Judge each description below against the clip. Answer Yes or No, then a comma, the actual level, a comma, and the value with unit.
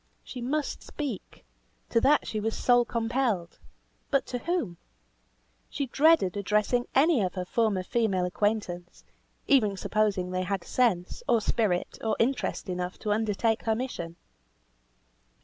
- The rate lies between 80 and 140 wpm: Yes, slow, 135 wpm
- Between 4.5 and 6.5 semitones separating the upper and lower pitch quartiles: Yes, average, 5.0 semitones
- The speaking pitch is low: No, high, 220 Hz